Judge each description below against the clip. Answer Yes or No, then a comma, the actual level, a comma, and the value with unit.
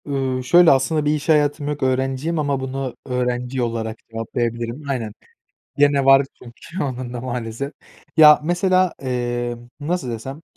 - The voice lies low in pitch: Yes, low, 130 Hz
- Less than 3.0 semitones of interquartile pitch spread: No, average, 3.3 semitones